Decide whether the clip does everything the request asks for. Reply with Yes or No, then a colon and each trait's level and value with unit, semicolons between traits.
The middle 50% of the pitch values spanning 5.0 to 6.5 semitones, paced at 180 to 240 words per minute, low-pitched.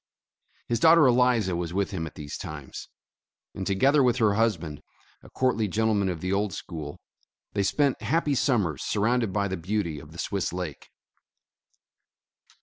No: wide, 5.6 semitones; average, 155 wpm; low, 100 Hz